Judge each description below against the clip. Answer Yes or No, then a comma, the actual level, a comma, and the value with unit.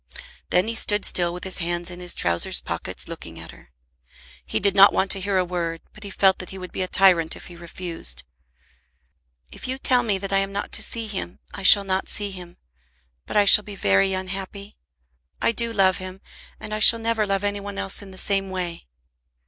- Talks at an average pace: No, fast, 220 wpm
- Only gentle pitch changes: Yes, narrow, 2.2 semitones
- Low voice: No, high, 190 Hz